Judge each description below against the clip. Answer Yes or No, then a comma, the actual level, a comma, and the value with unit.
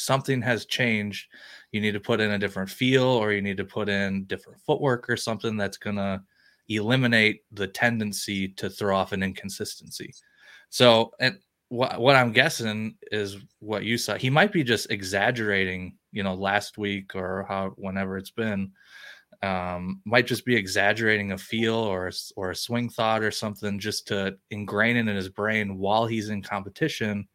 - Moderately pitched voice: No, low, 105 Hz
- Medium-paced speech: Yes, average, 175 wpm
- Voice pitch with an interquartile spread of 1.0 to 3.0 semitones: Yes, average, 2.7 semitones